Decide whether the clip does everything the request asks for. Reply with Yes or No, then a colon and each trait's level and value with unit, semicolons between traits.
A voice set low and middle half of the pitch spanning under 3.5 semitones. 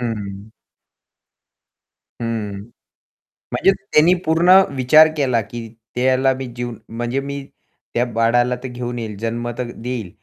Yes: low, 120 Hz; narrow, 2.4 semitones